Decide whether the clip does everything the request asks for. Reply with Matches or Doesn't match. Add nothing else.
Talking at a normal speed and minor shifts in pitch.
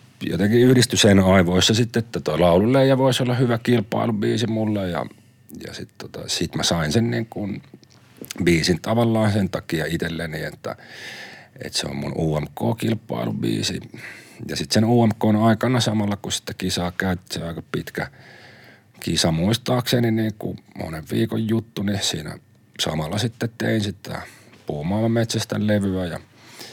Doesn't match